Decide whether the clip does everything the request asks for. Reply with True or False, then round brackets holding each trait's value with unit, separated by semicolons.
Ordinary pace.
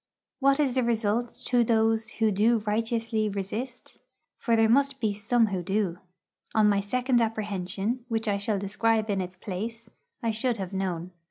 True (170 wpm)